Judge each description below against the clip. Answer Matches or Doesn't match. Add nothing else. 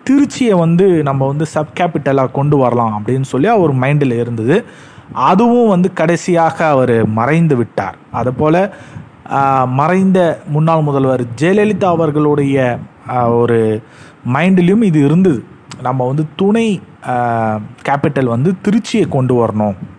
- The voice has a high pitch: Doesn't match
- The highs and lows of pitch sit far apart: Matches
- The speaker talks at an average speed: Matches